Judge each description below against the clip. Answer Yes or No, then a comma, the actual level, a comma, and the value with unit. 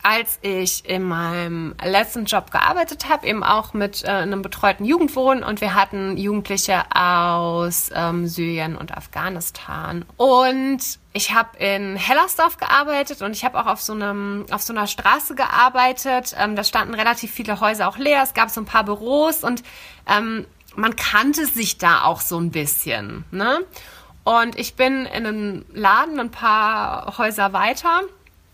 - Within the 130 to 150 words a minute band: No, average, 160 wpm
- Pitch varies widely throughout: No, average, 4.5 semitones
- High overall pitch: Yes, high, 215 Hz